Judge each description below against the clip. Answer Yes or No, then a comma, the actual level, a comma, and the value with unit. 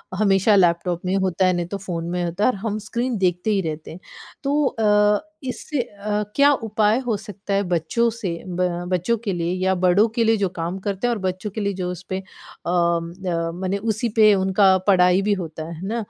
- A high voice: Yes, high, 195 Hz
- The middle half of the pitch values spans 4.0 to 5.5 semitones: No, average, 3.1 semitones